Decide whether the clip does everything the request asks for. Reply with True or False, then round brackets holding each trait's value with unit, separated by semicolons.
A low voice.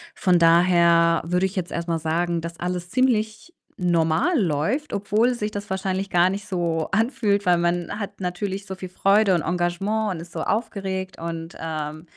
False (180 Hz)